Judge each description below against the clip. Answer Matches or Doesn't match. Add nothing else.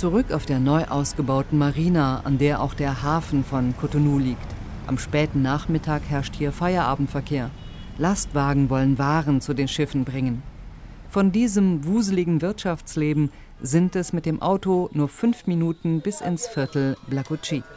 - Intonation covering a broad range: Doesn't match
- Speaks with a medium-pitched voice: Matches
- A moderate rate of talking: Matches